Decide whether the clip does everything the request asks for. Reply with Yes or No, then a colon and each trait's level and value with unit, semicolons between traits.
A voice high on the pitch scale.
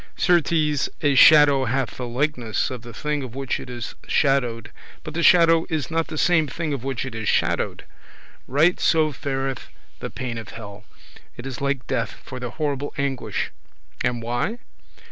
No: low, 135 Hz